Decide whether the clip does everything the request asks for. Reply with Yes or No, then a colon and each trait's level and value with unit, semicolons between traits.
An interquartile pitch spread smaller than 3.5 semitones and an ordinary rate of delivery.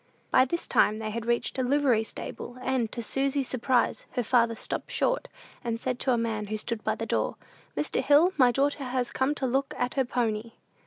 No: narrow, 2.6 semitones; fast, 210 wpm